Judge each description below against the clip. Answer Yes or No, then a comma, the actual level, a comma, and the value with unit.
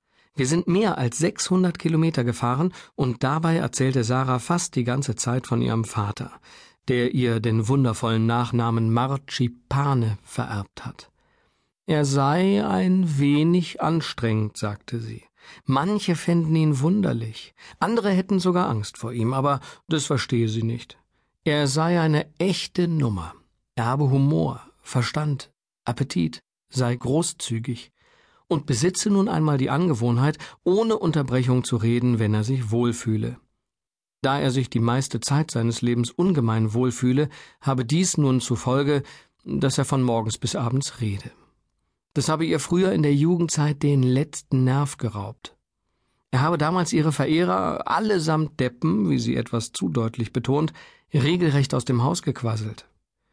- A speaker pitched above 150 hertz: No, low, 135 Hz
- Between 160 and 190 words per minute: No, average, 140 wpm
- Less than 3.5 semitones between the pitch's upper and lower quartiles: No, average, 5.0 semitones